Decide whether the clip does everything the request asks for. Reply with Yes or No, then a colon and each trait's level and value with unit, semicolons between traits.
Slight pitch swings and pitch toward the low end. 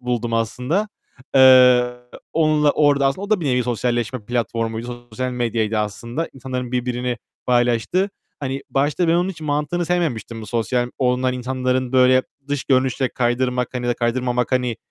Yes: narrow, 2.1 semitones; low, 125 Hz